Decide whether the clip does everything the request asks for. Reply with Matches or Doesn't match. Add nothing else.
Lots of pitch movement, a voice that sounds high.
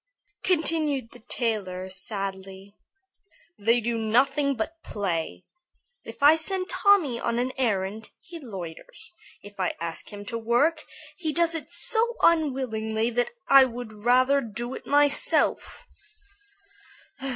Matches